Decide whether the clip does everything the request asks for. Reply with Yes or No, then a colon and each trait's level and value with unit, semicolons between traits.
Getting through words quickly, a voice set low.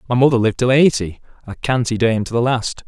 Yes: fast, 230 wpm; low, 120 Hz